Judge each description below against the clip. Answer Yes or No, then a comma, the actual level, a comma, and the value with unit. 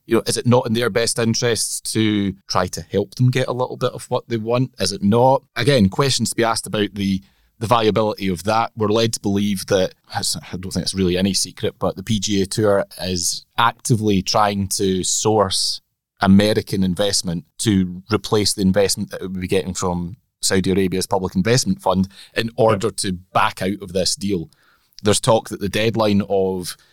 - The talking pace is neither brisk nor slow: Yes, average, 195 wpm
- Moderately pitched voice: No, low, 100 Hz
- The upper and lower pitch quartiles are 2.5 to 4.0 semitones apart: Yes, average, 3.2 semitones